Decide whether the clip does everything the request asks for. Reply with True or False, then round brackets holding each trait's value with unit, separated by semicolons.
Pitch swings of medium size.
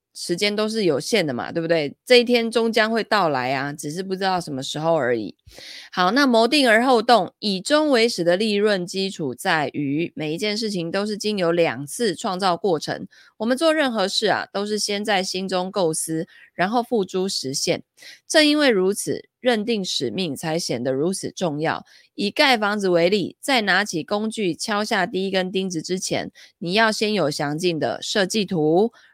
True (4.6 semitones)